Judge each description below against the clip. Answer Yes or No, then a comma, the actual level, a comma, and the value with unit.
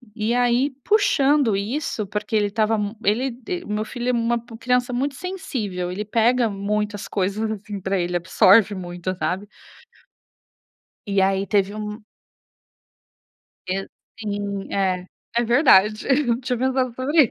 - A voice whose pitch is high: Yes, high, 215 Hz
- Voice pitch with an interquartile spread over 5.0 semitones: No, average, 3.8 semitones